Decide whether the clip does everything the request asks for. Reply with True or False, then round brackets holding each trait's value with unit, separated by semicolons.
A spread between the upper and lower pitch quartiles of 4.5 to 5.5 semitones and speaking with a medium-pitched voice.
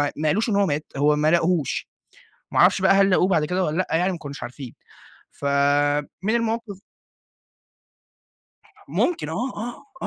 True (5.0 semitones; 180 Hz)